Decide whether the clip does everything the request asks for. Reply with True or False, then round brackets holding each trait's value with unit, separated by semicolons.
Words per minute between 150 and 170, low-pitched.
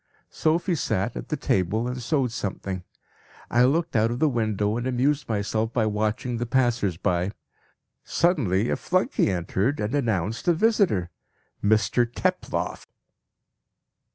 False (135 wpm; 115 Hz)